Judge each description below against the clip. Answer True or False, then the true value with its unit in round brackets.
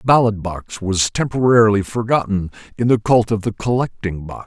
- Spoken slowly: False (175 wpm)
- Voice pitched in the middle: False (105 Hz)